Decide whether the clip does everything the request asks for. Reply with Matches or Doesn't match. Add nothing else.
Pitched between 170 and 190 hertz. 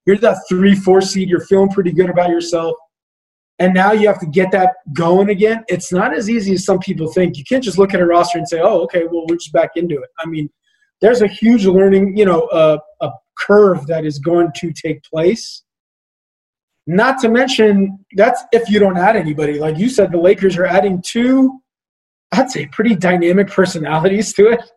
Matches